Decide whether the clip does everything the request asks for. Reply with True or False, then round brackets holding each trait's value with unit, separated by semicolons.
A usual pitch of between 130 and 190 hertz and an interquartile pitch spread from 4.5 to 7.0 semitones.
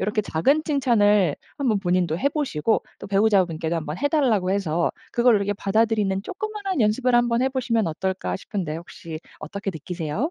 False (205 Hz; 5.6 semitones)